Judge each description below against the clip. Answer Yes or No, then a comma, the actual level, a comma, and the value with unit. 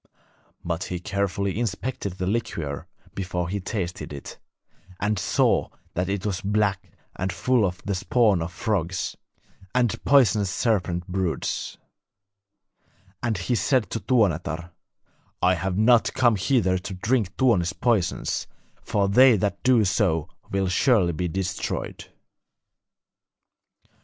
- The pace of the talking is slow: Yes, slow, 125 wpm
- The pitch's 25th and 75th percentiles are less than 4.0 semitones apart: Yes, average, 3.6 semitones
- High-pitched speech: No, very low, 95 Hz